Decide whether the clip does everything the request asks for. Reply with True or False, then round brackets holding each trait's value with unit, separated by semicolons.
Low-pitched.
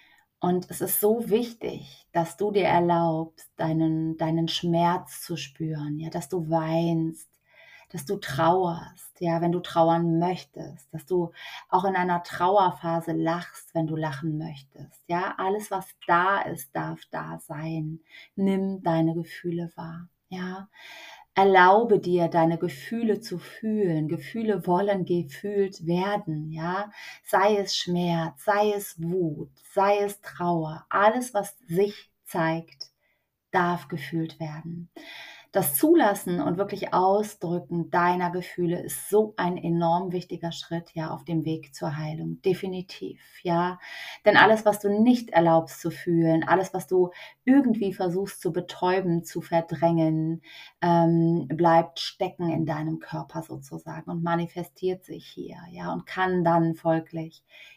False (175 Hz)